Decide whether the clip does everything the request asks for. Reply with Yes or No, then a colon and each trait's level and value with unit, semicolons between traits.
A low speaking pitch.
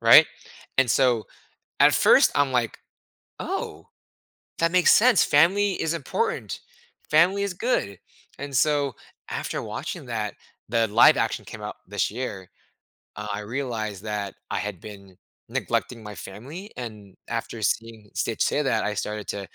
Yes: low, 115 Hz